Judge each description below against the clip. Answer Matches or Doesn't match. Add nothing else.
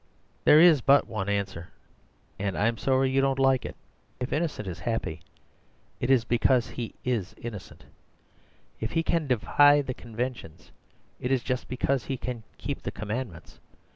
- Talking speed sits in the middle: Matches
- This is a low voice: Matches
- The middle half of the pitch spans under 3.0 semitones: Doesn't match